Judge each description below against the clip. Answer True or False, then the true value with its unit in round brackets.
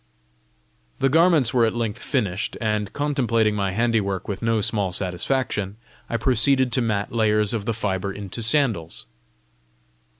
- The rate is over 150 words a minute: False (140 wpm)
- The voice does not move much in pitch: False (3.3 semitones)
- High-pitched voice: False (110 Hz)